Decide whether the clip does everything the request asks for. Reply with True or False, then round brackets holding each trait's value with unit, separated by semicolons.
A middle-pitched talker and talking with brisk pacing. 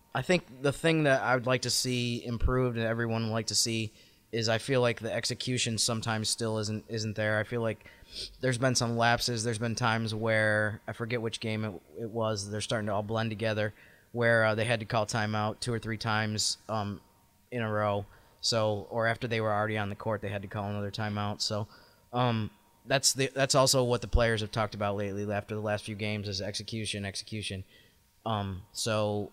False (110 Hz; 215 wpm)